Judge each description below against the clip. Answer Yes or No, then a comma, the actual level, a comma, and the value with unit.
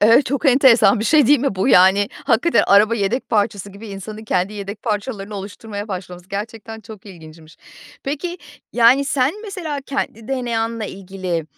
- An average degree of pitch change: Yes, average, 4.6 semitones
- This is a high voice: Yes, high, 215 Hz